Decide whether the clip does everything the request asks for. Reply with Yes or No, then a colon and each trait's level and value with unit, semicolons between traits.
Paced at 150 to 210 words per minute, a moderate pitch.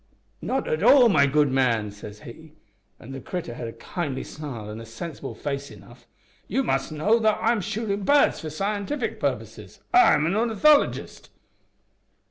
Yes: average, 170 wpm; medium, 155 Hz